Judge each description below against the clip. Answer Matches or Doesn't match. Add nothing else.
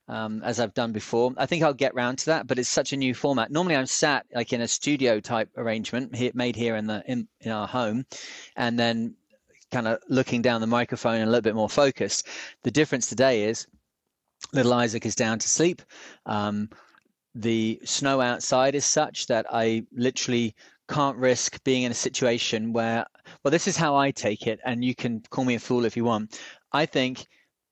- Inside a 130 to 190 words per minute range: Doesn't match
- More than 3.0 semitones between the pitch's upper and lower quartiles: Doesn't match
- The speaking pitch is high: Doesn't match